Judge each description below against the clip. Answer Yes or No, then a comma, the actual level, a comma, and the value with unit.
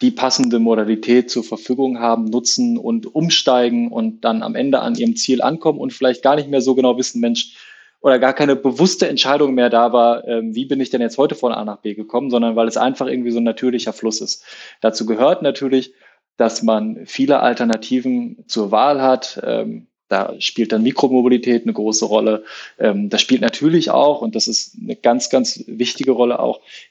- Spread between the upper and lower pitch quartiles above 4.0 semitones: No, average, 3.4 semitones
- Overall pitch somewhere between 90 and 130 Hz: Yes, low, 125 Hz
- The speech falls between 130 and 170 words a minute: No, fast, 190 wpm